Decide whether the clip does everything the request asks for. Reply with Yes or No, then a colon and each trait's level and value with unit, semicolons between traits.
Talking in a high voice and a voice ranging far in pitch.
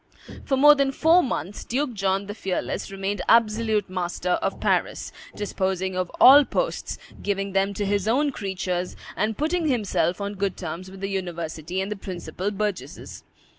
No: high, 200 Hz; average, 3.3 semitones